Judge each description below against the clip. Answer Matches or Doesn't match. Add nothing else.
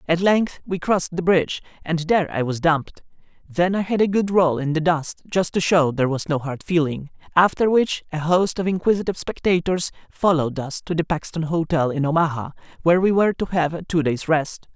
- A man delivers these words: Matches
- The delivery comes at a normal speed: Doesn't match